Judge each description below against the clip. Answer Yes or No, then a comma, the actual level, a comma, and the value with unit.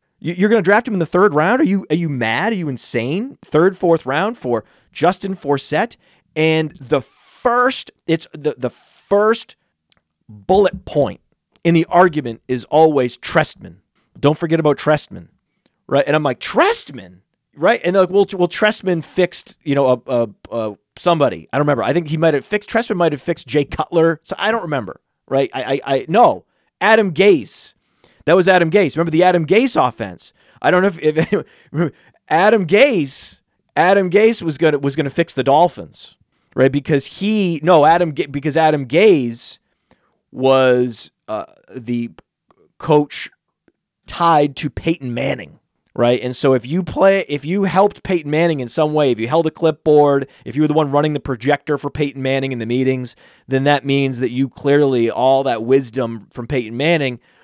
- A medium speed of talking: Yes, average, 180 wpm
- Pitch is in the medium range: Yes, medium, 155 Hz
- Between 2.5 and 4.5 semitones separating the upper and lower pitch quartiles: No, average, 5.0 semitones